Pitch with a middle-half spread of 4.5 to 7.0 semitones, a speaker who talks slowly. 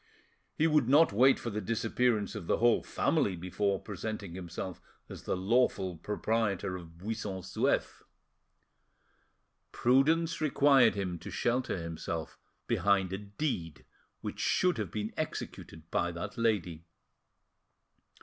Yes: average, 5.0 semitones; slow, 125 wpm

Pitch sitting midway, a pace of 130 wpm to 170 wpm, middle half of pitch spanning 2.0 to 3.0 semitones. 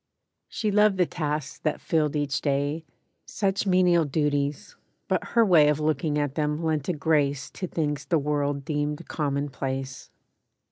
Yes: medium, 150 Hz; average, 150 wpm; narrow, 2.4 semitones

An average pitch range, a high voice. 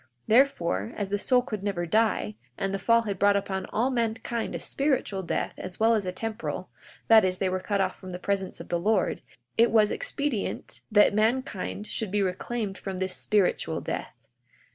Yes: average, 3.3 semitones; high, 205 Hz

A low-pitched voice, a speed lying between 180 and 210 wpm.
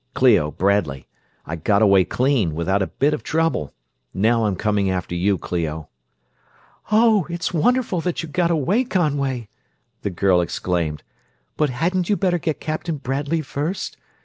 No: low, 130 Hz; average, 150 wpm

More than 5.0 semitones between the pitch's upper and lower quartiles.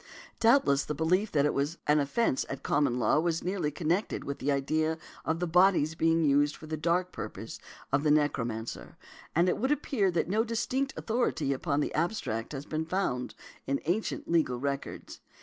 No: average, 4.4 semitones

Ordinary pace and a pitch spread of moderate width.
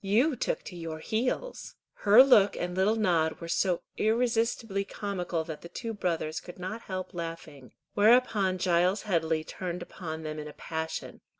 Yes: average, 165 wpm; average, 4.6 semitones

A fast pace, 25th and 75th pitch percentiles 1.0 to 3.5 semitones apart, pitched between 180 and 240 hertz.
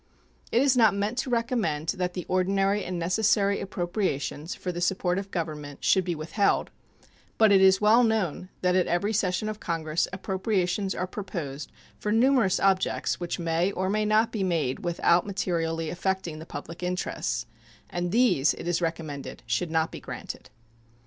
No: average, 170 wpm; average, 3.2 semitones; medium, 185 Hz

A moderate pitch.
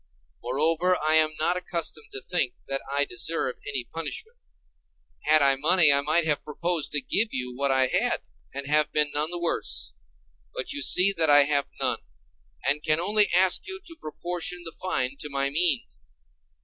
Yes: medium, 155 Hz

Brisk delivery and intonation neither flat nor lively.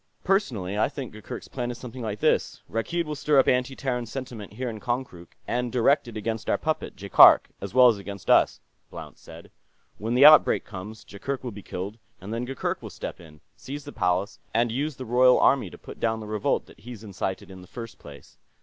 Yes: fast, 215 wpm; average, 3.9 semitones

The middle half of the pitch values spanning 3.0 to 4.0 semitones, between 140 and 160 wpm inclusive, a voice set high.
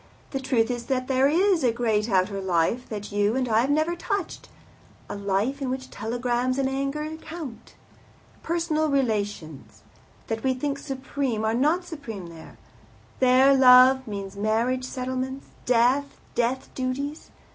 Yes: average, 3.7 semitones; average, 145 wpm; very high, 255 Hz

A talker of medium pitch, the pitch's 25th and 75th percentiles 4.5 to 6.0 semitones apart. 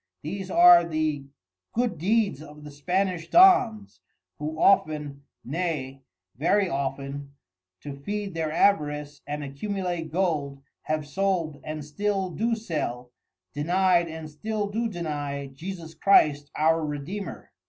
Yes: medium, 160 Hz; average, 4.8 semitones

